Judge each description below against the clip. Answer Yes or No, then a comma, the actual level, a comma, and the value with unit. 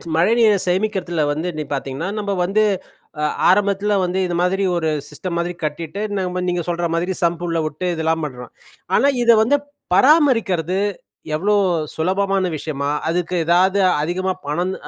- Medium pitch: Yes, medium, 180 Hz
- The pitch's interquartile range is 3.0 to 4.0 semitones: Yes, average, 3.3 semitones